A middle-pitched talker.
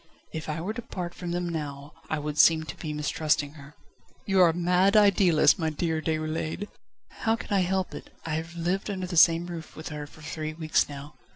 Yes: medium, 165 Hz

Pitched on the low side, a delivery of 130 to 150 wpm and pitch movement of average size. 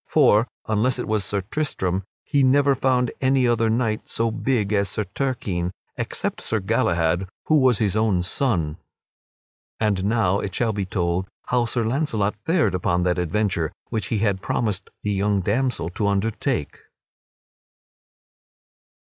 Yes: low, 105 Hz; average, 145 wpm; average, 4.4 semitones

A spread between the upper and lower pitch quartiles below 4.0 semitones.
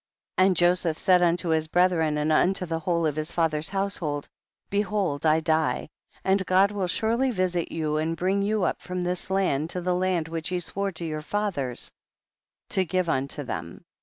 Yes: average, 3.1 semitones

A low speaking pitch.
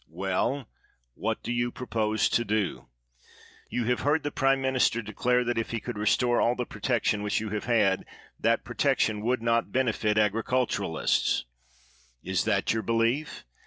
Yes: low, 115 Hz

